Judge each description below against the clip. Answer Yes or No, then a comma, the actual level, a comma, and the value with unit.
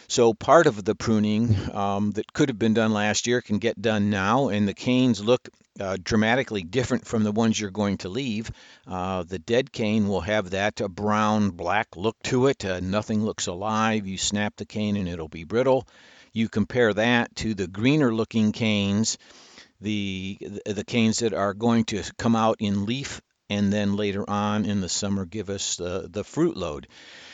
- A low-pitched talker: Yes, low, 105 Hz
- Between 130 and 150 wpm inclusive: No, average, 190 wpm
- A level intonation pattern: Yes, narrow, 2.1 semitones